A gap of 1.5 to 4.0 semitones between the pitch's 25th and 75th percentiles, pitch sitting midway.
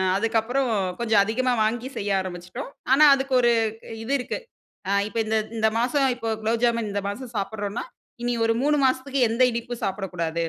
No: average, 3.7 semitones; high, 230 Hz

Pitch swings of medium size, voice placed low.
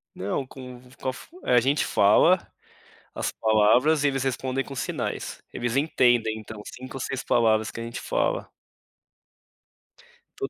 Yes: average, 3.2 semitones; low, 125 Hz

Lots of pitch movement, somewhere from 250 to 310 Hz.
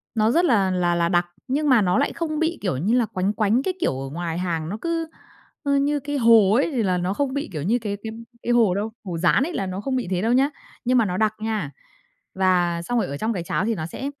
No: wide, 6.3 semitones; high, 215 Hz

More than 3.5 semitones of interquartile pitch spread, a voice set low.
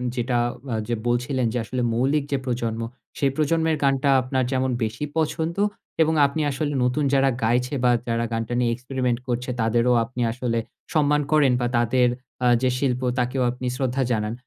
No: narrow, 2.4 semitones; low, 125 Hz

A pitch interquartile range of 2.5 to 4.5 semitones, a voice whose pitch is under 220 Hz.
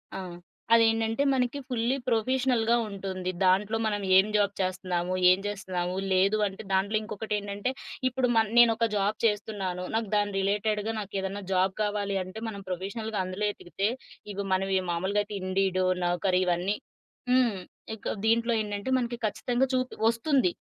Yes: average, 2.8 semitones; high, 205 Hz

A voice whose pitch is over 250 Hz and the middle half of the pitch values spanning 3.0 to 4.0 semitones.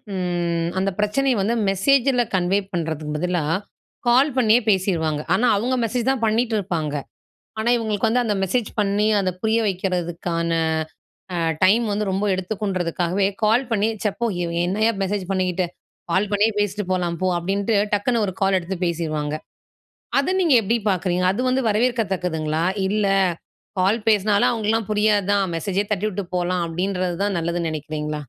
No: high, 195 Hz; average, 3.7 semitones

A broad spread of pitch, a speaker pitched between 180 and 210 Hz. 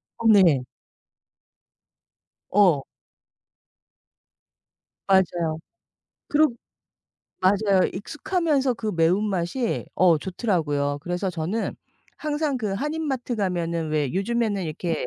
Yes: wide, 5.9 semitones; high, 190 Hz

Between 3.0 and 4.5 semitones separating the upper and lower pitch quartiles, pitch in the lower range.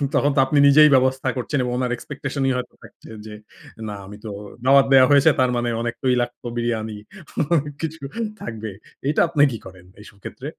Yes: average, 3.3 semitones; low, 130 Hz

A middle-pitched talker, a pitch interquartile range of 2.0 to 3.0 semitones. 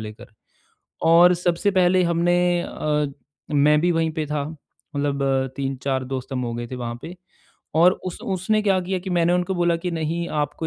No: medium, 165 Hz; average, 4.2 semitones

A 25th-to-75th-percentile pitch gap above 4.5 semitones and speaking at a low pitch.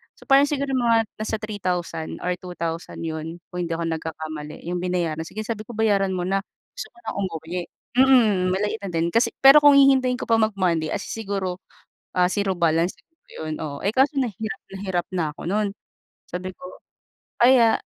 No: average, 5.0 semitones; high, 190 Hz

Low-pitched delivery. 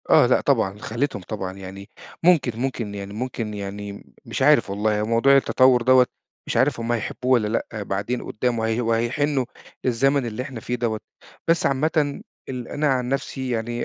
Yes: low, 120 Hz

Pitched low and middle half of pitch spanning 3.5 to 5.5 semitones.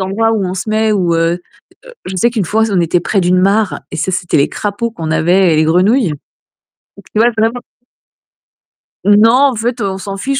No: high, 195 Hz; average, 4.0 semitones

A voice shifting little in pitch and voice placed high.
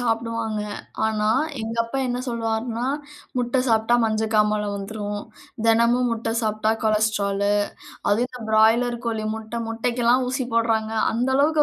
Yes: narrow, 1.8 semitones; high, 225 Hz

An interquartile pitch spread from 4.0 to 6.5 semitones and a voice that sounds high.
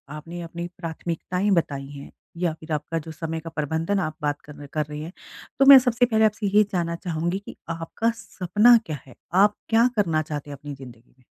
No: average, 5.0 semitones; medium, 165 Hz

